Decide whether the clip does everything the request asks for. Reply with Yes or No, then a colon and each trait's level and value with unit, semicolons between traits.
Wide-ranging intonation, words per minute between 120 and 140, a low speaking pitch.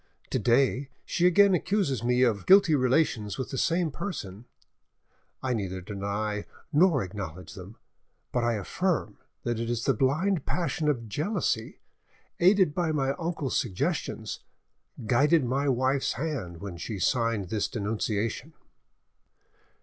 Yes: wide, 6.8 semitones; slow, 135 wpm; low, 125 Hz